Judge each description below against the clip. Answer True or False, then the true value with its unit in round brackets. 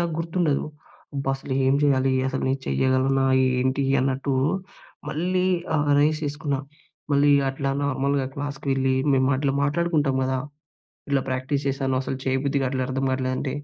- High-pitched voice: False (135 Hz)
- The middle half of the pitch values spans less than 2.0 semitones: True (1.6 semitones)